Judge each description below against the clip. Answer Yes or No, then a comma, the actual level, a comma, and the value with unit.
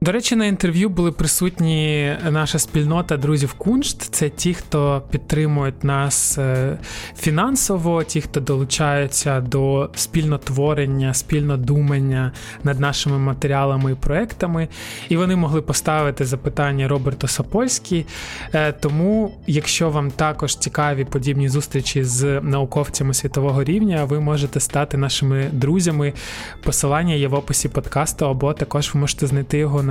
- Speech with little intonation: Yes, narrow, 2.2 semitones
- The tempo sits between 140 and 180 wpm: No, average, 125 wpm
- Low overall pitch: No, medium, 145 Hz